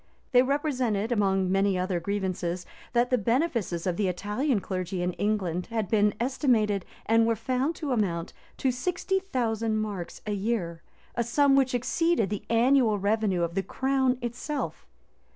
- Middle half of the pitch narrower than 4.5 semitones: No, average, 4.8 semitones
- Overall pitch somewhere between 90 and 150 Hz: No, high, 220 Hz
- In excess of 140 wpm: Yes, average, 155 wpm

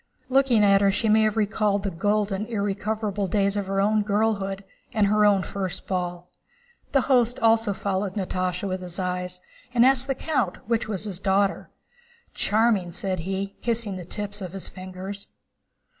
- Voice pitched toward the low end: No, high, 200 Hz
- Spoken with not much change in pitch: Yes, narrow, 2.3 semitones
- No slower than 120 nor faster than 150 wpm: No, average, 170 wpm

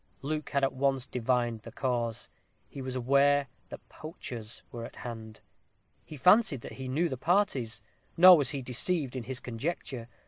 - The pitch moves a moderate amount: Yes, average, 3.3 semitones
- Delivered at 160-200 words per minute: Yes, average, 170 wpm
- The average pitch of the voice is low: Yes, low, 130 Hz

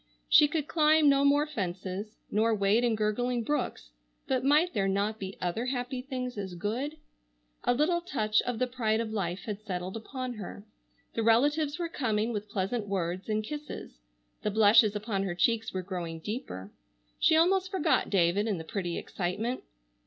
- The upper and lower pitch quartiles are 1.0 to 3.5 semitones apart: No, average, 4.9 semitones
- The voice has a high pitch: Yes, high, 220 Hz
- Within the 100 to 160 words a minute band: No, average, 175 wpm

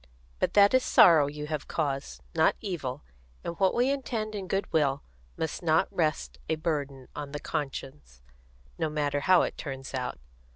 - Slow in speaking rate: No, average, 165 wpm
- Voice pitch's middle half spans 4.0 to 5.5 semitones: Yes, average, 4.5 semitones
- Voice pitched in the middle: Yes, medium, 150 Hz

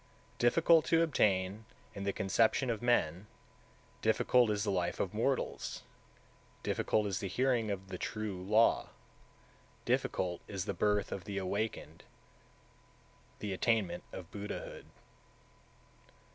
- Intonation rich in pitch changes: No, average, 3.1 semitones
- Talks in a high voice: No, low, 105 Hz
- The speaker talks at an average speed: No, slow, 125 wpm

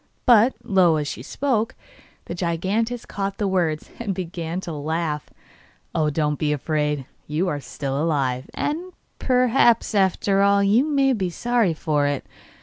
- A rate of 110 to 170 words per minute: Yes, average, 150 wpm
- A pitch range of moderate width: No, wide, 6.7 semitones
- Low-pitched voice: No, medium, 180 Hz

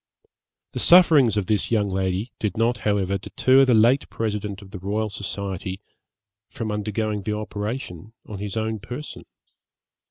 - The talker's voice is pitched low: Yes, low, 105 Hz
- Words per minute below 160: Yes, average, 150 wpm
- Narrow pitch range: Yes, narrow, 2.3 semitones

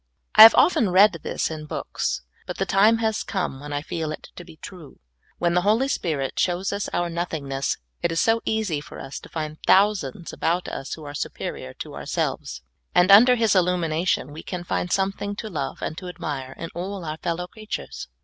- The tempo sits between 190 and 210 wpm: Yes, average, 200 wpm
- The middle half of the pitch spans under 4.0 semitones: No, average, 4.5 semitones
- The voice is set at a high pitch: No, medium, 175 Hz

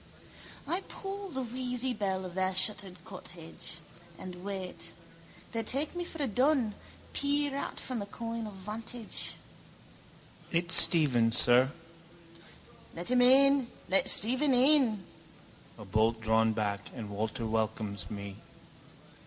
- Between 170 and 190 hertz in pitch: No, high, 200 Hz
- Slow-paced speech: Yes, slow, 130 wpm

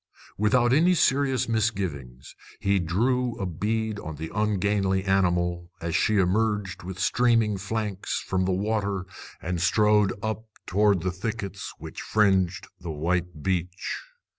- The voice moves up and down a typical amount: Yes, average, 3.4 semitones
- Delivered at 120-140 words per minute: Yes, slow, 135 wpm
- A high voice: No, low, 100 Hz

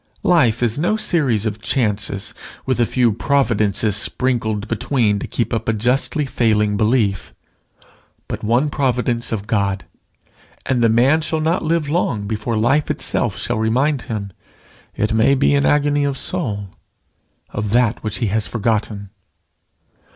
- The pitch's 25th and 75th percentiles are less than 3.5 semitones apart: No, average, 4.4 semitones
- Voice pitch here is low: Yes, low, 115 Hz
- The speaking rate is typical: Yes, average, 150 wpm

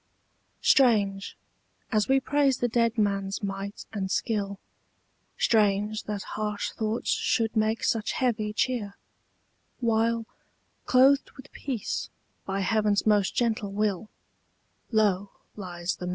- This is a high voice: Yes, high, 215 Hz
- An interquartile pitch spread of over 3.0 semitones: No, narrow, 2.6 semitones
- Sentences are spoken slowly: Yes, slow, 120 wpm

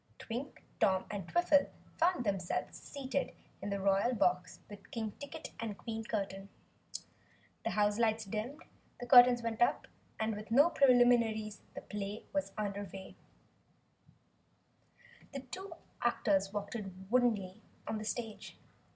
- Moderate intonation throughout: Yes, average, 3.5 semitones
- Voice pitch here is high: Yes, high, 220 Hz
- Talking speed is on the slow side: Yes, slow, 130 wpm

